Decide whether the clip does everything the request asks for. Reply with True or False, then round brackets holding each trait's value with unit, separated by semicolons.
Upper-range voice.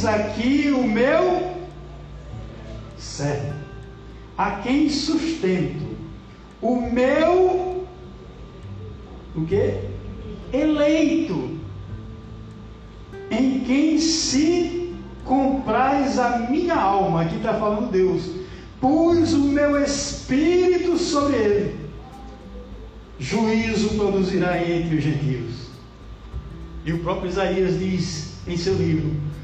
True (195 Hz)